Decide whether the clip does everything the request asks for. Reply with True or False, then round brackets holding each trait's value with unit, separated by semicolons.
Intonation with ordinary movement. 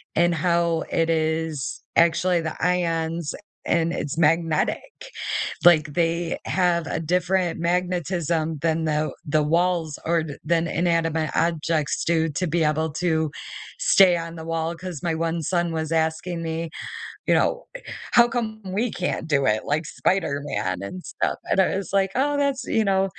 False (2.1 semitones)